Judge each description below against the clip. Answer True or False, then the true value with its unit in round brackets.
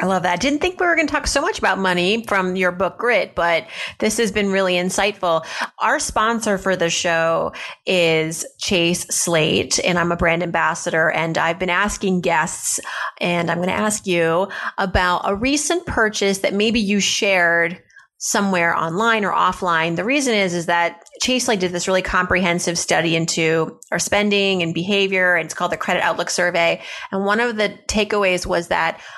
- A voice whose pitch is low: False (185 Hz)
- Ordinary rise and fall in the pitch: True (3.3 semitones)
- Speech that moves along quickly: False (190 wpm)